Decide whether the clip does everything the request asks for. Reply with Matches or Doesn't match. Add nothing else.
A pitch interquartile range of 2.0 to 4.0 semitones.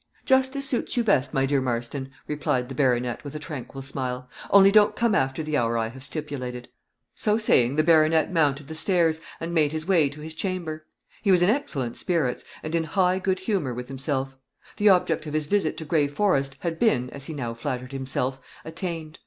Doesn't match